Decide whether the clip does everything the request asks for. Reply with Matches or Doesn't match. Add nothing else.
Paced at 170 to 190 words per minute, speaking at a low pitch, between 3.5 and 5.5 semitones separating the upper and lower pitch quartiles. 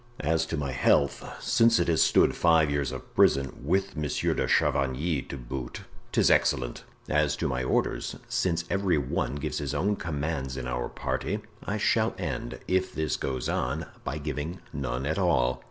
Matches